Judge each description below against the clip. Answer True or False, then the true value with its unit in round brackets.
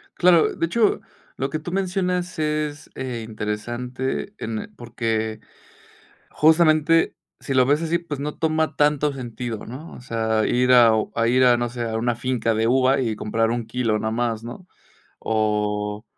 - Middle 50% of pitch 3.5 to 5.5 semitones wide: True (5.2 semitones)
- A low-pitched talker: True (125 Hz)